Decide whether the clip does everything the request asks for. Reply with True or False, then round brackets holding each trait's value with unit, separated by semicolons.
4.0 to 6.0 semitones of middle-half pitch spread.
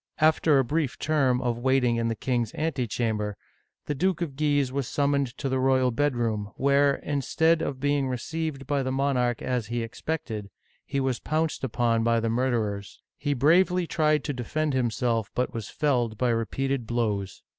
False (3.6 semitones)